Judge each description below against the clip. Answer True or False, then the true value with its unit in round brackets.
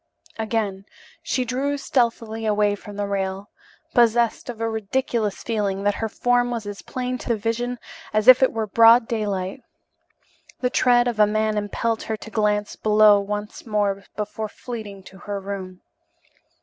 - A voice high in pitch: True (215 Hz)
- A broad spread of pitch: False (2.6 semitones)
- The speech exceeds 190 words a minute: False (160 wpm)